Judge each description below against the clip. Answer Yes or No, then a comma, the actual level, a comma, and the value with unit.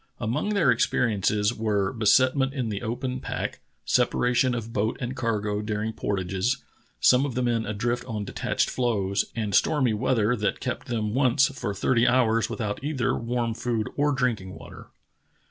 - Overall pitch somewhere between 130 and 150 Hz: No, low, 115 Hz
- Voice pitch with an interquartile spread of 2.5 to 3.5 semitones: Yes, average, 3.2 semitones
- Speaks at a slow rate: No, average, 165 wpm